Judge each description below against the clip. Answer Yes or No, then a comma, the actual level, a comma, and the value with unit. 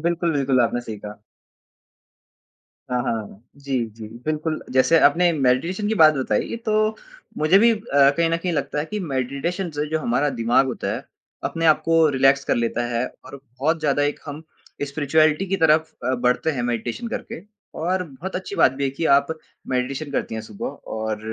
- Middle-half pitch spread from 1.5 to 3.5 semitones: No, average, 4.6 semitones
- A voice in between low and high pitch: Yes, medium, 145 Hz